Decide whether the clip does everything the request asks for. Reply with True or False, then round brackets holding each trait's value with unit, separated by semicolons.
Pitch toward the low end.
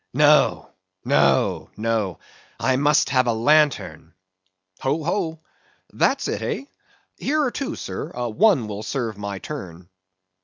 True (130 Hz)